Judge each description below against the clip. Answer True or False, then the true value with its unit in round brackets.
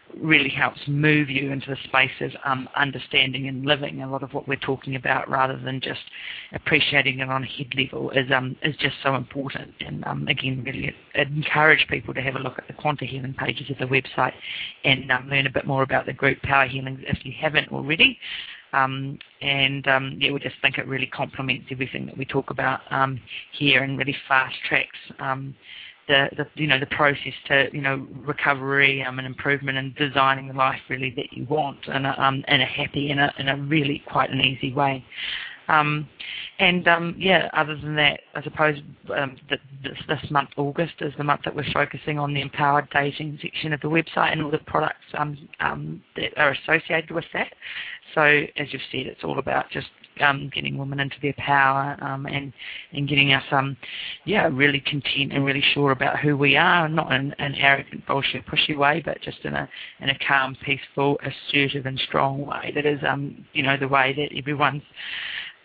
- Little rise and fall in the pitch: True (1.5 semitones)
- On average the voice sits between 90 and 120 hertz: False (140 Hz)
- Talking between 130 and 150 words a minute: False (200 wpm)